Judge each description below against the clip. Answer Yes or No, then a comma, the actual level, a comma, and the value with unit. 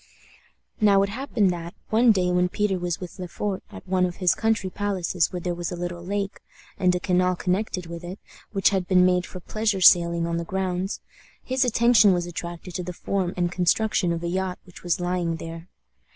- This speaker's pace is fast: Yes, fast, 210 wpm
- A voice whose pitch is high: No, medium, 180 Hz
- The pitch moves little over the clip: Yes, narrow, 2.1 semitones